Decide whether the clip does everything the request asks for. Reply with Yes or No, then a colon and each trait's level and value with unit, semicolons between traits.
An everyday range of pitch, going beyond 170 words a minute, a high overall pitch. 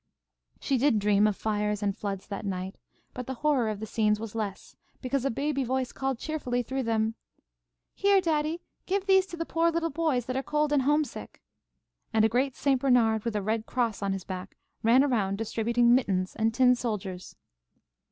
Yes: average, 4.7 semitones; average, 190 wpm; high, 240 Hz